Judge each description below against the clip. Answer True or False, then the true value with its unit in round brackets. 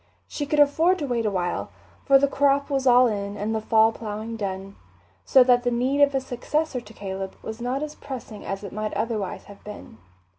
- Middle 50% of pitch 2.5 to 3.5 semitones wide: False (4.8 semitones)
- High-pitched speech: True (235 Hz)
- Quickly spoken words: True (215 wpm)